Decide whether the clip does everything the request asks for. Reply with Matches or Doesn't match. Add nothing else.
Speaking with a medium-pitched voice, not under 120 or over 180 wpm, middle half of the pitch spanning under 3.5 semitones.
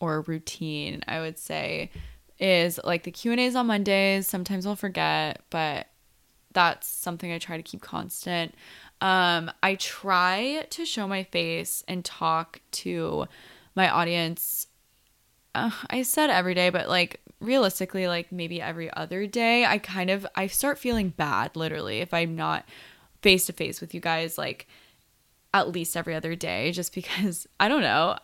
Matches